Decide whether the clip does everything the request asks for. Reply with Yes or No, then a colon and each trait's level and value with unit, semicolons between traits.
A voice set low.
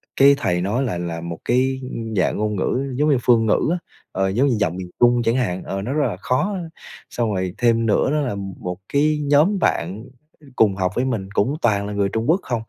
Yes: low, 115 Hz